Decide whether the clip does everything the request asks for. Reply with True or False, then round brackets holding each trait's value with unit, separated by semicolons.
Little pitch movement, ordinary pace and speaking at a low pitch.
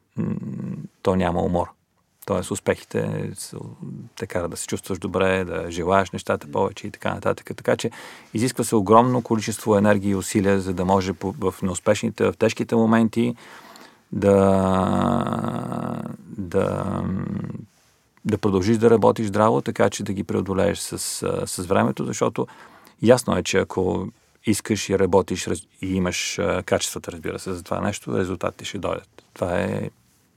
False (3.2 semitones; 140 wpm; 100 Hz)